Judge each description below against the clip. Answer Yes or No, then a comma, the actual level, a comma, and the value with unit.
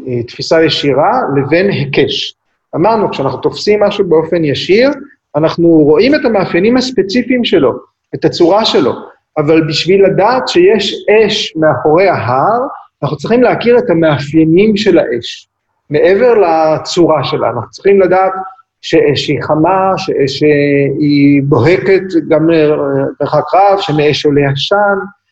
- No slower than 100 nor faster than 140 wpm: Yes, average, 125 wpm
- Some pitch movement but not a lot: Yes, average, 4.9 semitones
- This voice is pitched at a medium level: Yes, medium, 165 Hz